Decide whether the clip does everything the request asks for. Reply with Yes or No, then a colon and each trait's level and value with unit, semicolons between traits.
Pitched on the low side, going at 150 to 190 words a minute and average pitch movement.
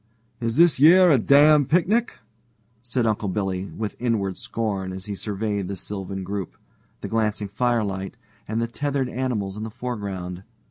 Yes: low, 110 Hz; average, 155 wpm; average, 4.3 semitones